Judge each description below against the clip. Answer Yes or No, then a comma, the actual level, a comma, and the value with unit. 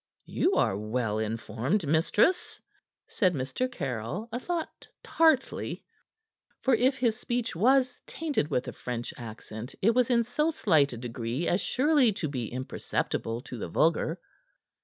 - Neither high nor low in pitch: Yes, medium, 170 Hz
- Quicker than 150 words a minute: No, average, 145 wpm